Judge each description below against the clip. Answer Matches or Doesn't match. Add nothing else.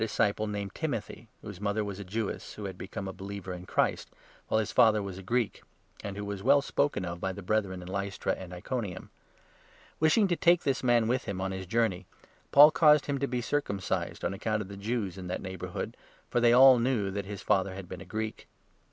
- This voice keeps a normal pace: Doesn't match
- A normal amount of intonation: Matches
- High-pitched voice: Doesn't match